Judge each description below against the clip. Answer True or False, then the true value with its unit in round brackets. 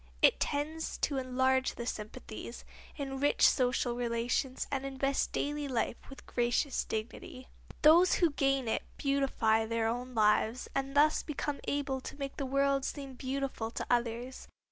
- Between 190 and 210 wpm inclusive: False (150 wpm)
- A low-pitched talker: False (265 Hz)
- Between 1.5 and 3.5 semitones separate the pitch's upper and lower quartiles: True (2.6 semitones)